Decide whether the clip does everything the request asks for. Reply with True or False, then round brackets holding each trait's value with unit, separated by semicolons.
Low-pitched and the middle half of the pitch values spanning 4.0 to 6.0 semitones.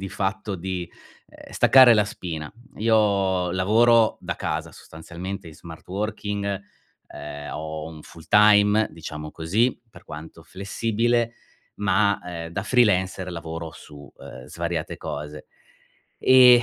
True (95 Hz; 4.6 semitones)